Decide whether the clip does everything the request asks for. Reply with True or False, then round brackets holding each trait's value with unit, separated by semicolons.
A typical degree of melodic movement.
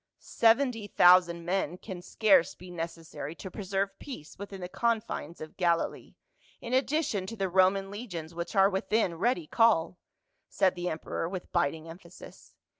True (3.2 semitones)